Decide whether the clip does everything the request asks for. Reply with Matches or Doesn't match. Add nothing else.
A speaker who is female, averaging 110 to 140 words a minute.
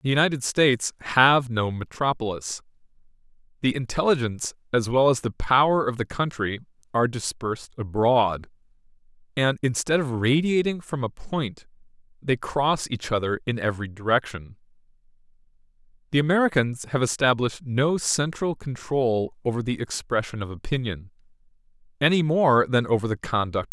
Doesn't match